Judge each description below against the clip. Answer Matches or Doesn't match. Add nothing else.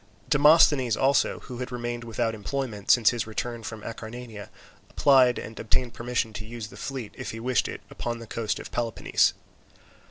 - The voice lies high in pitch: Doesn't match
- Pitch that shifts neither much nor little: Doesn't match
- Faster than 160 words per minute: Matches